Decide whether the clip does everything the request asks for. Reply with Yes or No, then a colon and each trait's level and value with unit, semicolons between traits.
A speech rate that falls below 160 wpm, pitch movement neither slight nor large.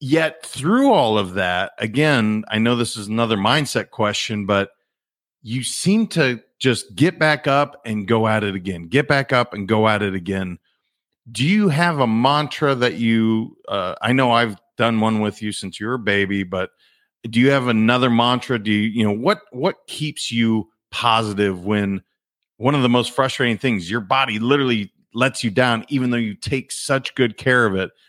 No: average, 195 wpm; average, 3.8 semitones